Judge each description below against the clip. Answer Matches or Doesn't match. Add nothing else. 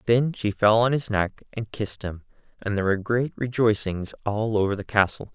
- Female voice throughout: Doesn't match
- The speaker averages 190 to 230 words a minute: Matches